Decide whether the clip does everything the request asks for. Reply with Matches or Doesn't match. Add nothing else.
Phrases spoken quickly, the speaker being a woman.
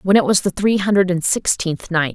Matches